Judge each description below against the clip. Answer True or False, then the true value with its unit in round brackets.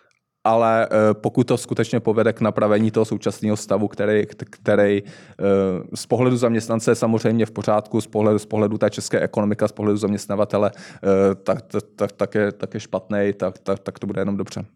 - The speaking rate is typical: False (180 wpm)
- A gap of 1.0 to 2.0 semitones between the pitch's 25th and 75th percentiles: True (1.7 semitones)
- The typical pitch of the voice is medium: False (105 Hz)